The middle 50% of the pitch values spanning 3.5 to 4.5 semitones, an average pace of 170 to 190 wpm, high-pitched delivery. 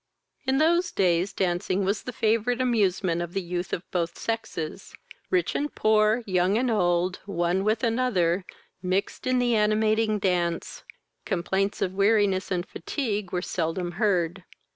No: average, 4.0 semitones; average, 145 wpm; high, 195 Hz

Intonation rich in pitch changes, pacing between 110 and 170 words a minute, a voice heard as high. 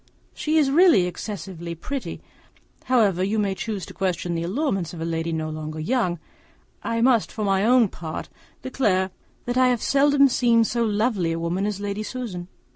No: wide, 5.9 semitones; average, 180 wpm; high, 205 Hz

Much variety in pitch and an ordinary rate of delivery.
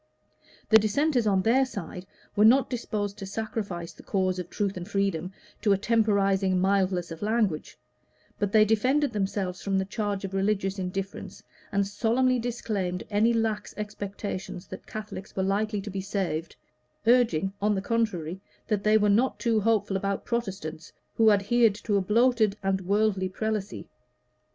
No: narrow, 2.4 semitones; average, 160 wpm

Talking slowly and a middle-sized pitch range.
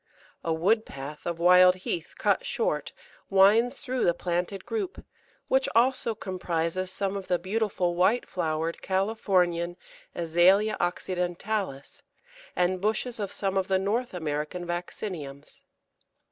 Yes: slow, 125 wpm; average, 3.6 semitones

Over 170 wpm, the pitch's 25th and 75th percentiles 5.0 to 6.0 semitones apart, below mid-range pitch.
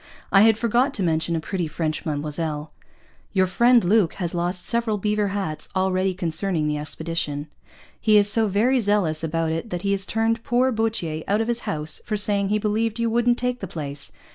No: average, 195 wpm; wide, 5.5 semitones; high, 195 Hz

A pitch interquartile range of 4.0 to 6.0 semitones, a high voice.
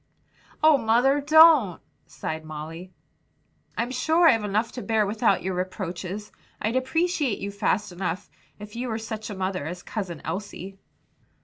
Yes: average, 5.0 semitones; high, 210 Hz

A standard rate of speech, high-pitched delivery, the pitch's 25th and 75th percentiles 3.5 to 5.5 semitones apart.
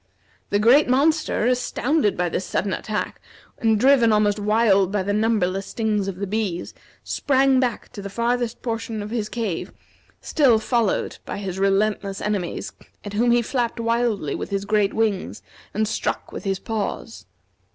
No: average, 160 wpm; high, 215 Hz; average, 3.0 semitones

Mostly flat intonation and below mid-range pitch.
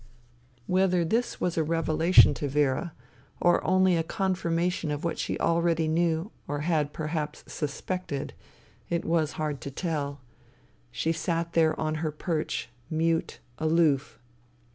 No: narrow, 2.1 semitones; medium, 165 Hz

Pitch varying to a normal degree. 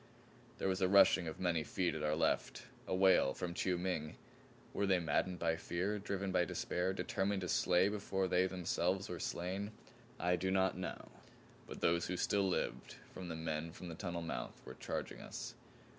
No: narrow, 1.9 semitones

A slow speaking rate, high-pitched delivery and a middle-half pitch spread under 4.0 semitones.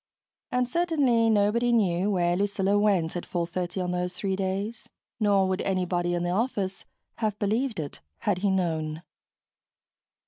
No: average, 145 wpm; high, 195 Hz; average, 3.1 semitones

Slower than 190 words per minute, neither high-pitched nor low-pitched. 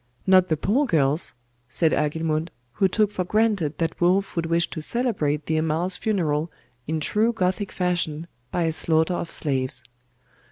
Yes: average, 160 wpm; medium, 170 Hz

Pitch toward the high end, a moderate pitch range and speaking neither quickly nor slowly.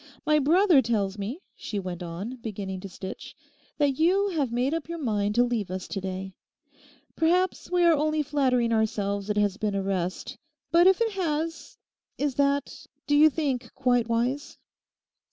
No: very high, 250 Hz; wide, 7.2 semitones; average, 170 wpm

